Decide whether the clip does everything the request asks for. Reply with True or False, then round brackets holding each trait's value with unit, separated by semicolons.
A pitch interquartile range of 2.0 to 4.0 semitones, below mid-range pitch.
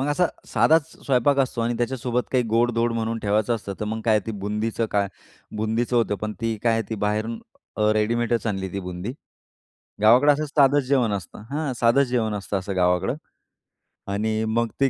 True (2.6 semitones; 115 Hz)